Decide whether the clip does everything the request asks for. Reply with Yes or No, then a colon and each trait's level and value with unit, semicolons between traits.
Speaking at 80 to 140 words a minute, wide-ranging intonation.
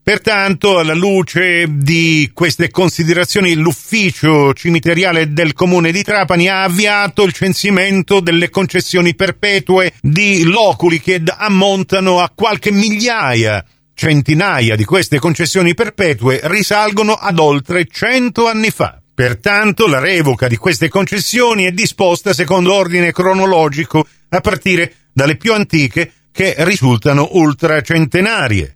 No: slow, 115 wpm; average, 3.7 semitones